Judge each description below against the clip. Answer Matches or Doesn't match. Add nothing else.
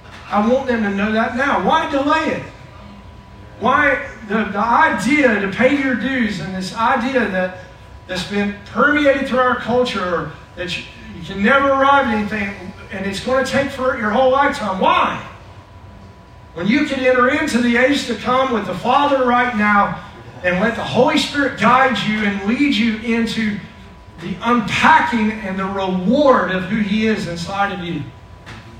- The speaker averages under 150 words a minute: Doesn't match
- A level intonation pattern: Doesn't match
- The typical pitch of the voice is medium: Doesn't match